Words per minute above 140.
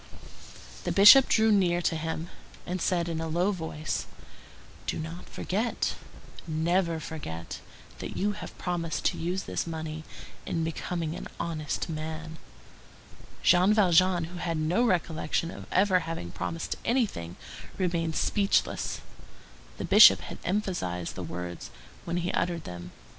No: slow, 135 wpm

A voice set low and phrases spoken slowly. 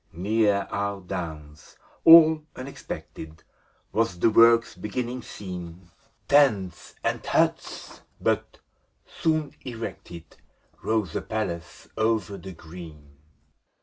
Yes: low, 100 Hz; slow, 100 wpm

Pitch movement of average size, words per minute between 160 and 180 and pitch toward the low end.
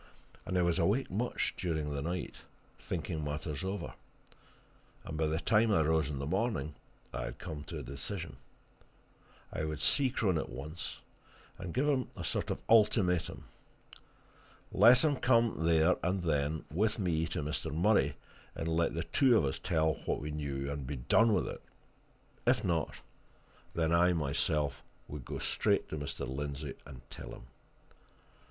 Yes: average, 4.4 semitones; average, 170 wpm; very low, 80 Hz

